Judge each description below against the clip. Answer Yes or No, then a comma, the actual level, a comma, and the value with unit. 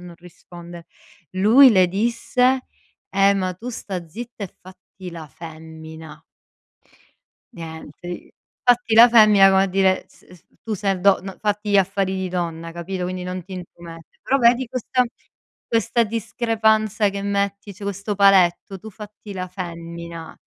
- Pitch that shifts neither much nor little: Yes, average, 3.5 semitones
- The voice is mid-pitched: No, high, 195 Hz